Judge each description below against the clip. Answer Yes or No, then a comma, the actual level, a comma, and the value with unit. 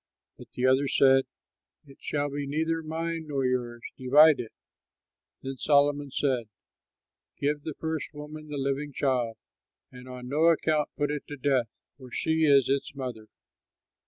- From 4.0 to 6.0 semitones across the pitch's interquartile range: No, narrow, 2.5 semitones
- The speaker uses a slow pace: No, average, 150 wpm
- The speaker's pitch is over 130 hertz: Yes, medium, 140 Hz